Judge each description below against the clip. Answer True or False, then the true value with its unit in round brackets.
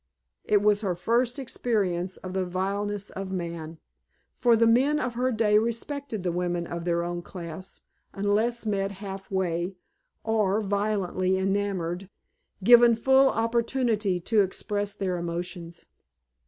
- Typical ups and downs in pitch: True (3.9 semitones)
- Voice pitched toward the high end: True (200 Hz)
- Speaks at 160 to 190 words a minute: False (135 wpm)